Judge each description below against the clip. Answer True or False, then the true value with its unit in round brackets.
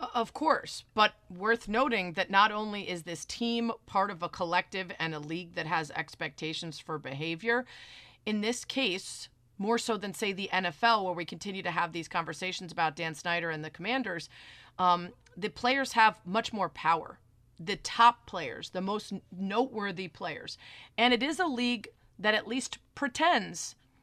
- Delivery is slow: False (170 wpm)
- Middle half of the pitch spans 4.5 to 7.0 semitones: True (5.1 semitones)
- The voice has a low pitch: False (195 Hz)